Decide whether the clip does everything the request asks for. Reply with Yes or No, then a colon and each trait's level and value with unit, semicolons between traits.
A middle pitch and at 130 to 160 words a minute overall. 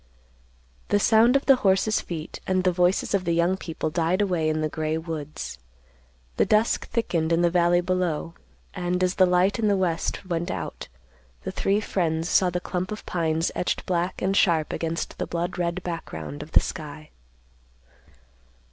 No: medium, 175 Hz; average, 175 wpm